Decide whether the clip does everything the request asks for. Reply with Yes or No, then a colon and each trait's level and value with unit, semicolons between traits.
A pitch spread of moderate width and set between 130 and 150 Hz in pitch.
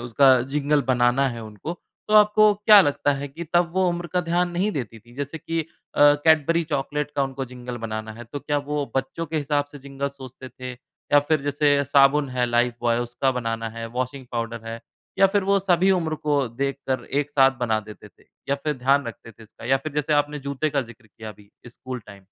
Yes: average, 3.7 semitones; medium, 140 Hz